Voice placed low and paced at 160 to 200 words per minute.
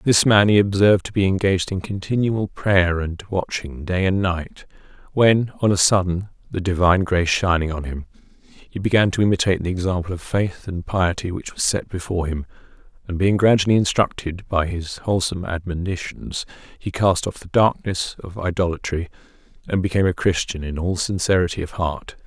Yes: very low, 95 Hz; average, 170 wpm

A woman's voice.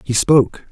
No: male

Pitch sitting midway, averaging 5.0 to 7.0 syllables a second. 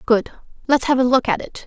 No: very high, 255 Hz; 6.0 syllables/s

